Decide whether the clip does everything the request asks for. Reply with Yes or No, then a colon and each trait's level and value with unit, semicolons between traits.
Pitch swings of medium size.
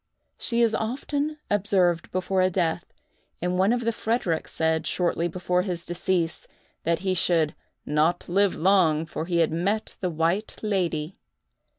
Yes: average, 3.3 semitones